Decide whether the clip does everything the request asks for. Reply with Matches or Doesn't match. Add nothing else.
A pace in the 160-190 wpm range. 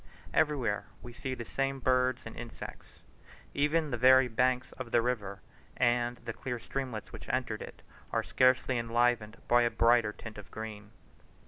Matches